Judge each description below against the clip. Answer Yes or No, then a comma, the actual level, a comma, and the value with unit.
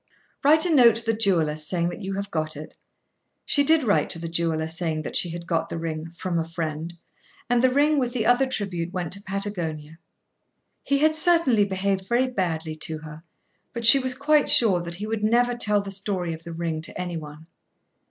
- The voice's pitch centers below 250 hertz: Yes, high, 190 Hz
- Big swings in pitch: Yes, wide, 6.5 semitones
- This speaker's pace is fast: Yes, fast, 210 wpm